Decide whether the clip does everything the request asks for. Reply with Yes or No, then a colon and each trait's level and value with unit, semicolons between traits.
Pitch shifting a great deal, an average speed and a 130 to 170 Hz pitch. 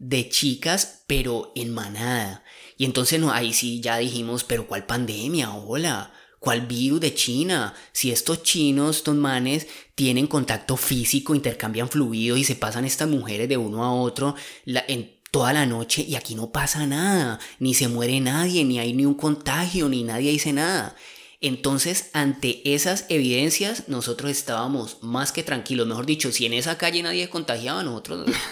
No: average, 3.8 semitones; average, 170 wpm; low, 135 Hz